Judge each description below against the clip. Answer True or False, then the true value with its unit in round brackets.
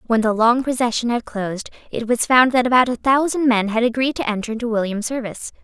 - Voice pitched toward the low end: False (235 Hz)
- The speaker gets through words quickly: True (225 wpm)